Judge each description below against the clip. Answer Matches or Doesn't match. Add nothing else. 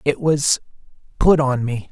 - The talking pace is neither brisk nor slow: Doesn't match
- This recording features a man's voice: Matches